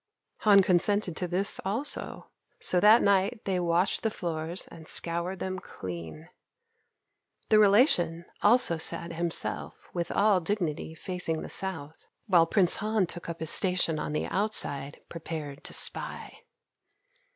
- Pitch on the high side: No, medium, 175 Hz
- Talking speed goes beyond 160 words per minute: No, average, 140 wpm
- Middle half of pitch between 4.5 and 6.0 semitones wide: No, average, 3.5 semitones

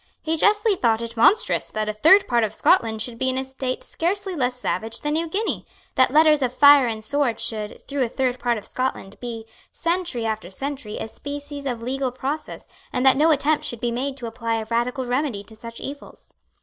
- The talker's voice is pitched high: Yes, very high, 255 Hz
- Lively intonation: No, average, 4.0 semitones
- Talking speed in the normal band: No, fast, 215 wpm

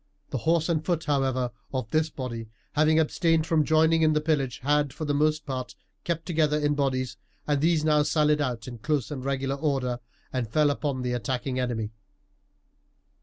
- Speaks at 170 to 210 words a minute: Yes, average, 180 wpm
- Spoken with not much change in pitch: No, average, 3.2 semitones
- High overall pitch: No, medium, 145 Hz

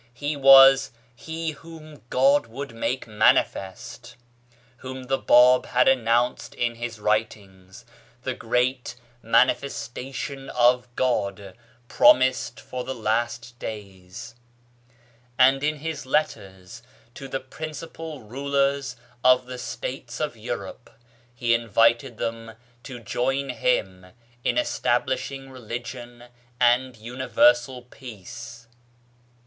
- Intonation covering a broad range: No, average, 2.7 semitones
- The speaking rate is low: Yes, slow, 105 wpm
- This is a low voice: Yes, low, 125 Hz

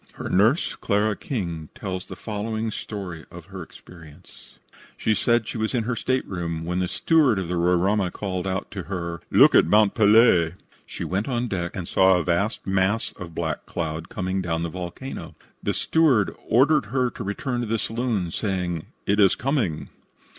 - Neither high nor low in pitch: No, very low, 95 Hz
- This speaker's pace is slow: No, average, 180 wpm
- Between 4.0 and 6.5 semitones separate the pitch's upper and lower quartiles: Yes, average, 4.3 semitones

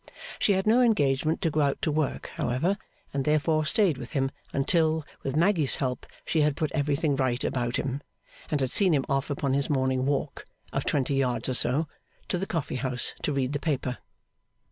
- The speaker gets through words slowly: No, average, 195 wpm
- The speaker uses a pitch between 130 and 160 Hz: Yes, medium, 140 Hz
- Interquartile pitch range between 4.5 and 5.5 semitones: No, average, 3.1 semitones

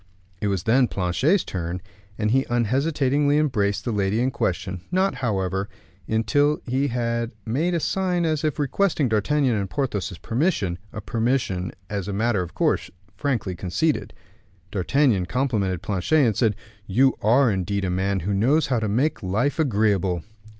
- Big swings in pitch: Yes, wide, 6.1 semitones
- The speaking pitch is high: No, low, 115 Hz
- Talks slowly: No, average, 155 wpm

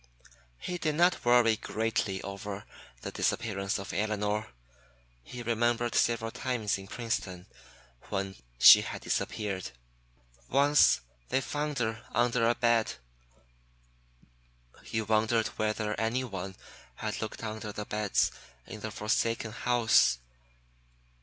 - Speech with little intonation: Yes, narrow, 2.3 semitones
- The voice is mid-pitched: No, low, 110 Hz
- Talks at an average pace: No, slow, 115 wpm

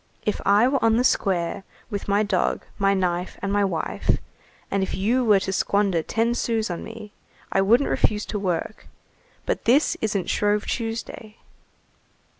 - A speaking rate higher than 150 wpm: Yes, average, 165 wpm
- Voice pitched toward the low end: No, high, 205 Hz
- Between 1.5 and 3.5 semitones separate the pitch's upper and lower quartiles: Yes, average, 2.7 semitones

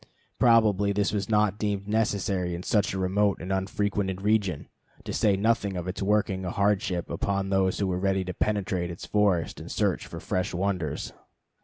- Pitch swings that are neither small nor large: No, narrow, 1.9 semitones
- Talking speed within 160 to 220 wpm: Yes, average, 180 wpm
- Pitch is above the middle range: No, low, 100 Hz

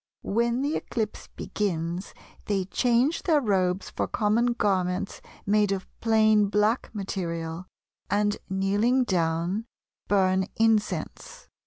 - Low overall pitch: No, high, 205 Hz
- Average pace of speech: No, slow, 110 wpm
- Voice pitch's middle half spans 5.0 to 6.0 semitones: No, average, 3.2 semitones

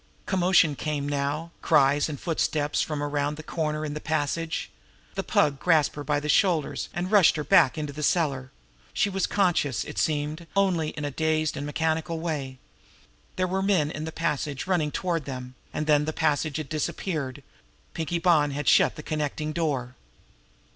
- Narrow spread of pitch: Yes, narrow, 2.3 semitones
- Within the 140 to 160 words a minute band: No, average, 175 wpm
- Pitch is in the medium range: Yes, medium, 155 Hz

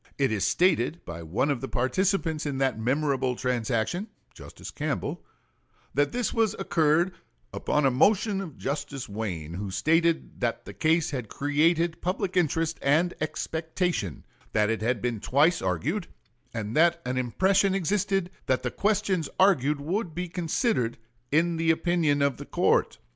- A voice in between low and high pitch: Yes, medium, 150 Hz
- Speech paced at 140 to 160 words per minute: Yes, average, 155 wpm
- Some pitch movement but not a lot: No, wide, 5.9 semitones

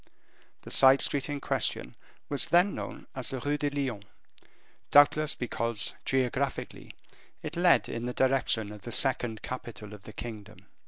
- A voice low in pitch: Yes, low, 130 Hz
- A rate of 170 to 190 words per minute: No, average, 155 wpm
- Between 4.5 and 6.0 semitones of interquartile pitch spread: No, average, 4.0 semitones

